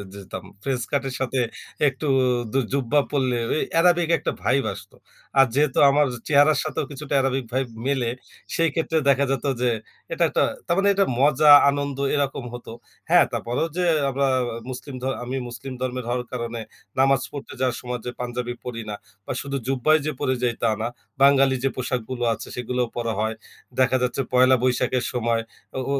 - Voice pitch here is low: Yes, low, 130 Hz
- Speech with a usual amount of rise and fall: No, narrow, 2.2 semitones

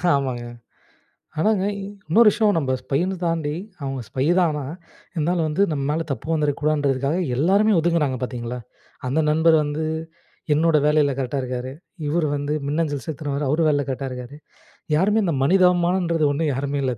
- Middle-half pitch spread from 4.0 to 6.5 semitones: No, average, 3.5 semitones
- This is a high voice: No, medium, 150 Hz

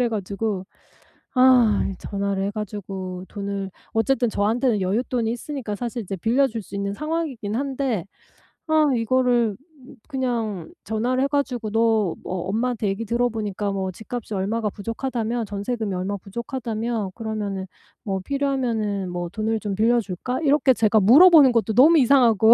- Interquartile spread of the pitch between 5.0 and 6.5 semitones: No, average, 3.7 semitones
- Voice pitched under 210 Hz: No, high, 225 Hz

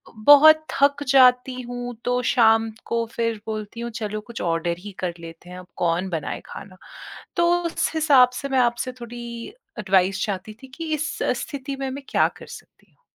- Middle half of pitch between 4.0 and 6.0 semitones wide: Yes, average, 4.7 semitones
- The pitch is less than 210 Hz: No, high, 235 Hz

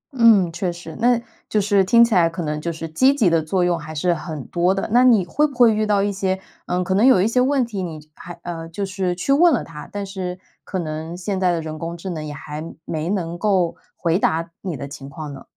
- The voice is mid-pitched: Yes, medium, 180 Hz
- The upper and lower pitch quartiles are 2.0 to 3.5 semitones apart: No, average, 3.9 semitones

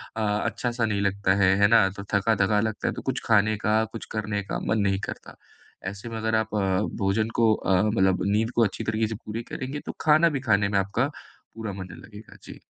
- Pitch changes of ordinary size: No, narrow, 2.0 semitones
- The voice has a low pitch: Yes, low, 110 Hz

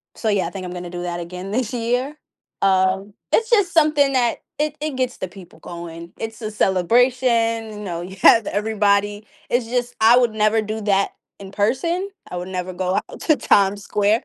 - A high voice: Yes, high, 210 Hz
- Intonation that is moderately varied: Yes, average, 4.6 semitones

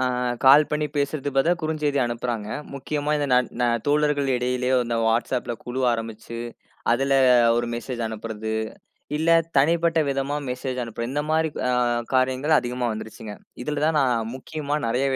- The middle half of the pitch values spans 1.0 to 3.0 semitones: No, average, 3.8 semitones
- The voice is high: No, low, 130 Hz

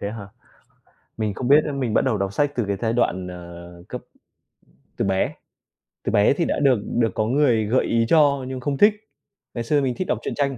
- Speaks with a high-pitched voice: No, low, 120 Hz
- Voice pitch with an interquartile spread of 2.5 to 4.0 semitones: No, average, 5.3 semitones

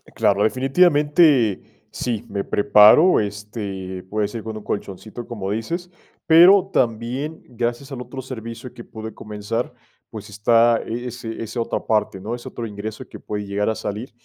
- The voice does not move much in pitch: No, average, 3.1 semitones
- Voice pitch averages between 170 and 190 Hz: No, low, 115 Hz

